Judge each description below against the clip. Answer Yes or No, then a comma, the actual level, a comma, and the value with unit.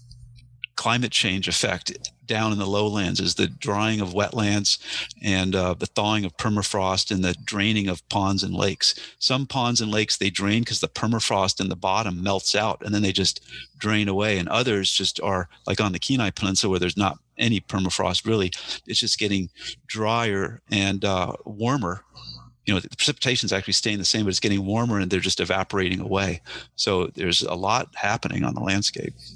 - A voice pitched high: No, low, 100 Hz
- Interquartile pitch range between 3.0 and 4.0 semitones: No, narrow, 2.6 semitones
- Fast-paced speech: No, average, 190 wpm